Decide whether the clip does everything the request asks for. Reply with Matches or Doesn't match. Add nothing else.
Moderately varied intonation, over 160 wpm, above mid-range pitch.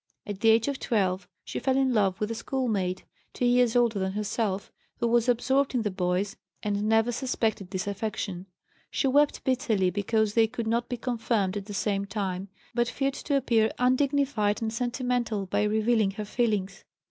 Matches